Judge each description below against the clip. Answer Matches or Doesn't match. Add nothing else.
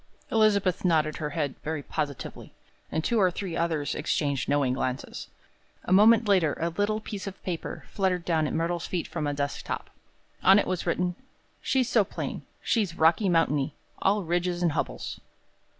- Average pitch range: Matches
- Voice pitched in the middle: Matches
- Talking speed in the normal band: Matches